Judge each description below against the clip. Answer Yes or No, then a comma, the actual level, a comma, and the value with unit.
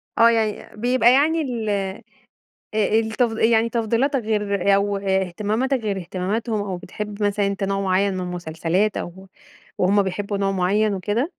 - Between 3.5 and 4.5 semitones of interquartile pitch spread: No, average, 2.7 semitones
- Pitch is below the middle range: No, high, 205 Hz